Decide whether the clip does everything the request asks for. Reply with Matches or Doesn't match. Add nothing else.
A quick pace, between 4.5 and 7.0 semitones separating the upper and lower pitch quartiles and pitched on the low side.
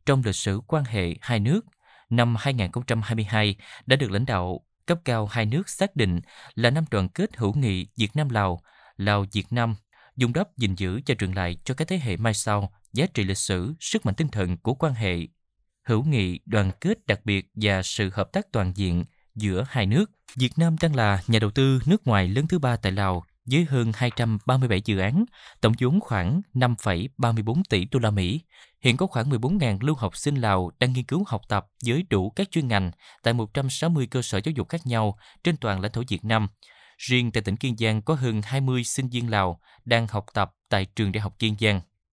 Doesn't match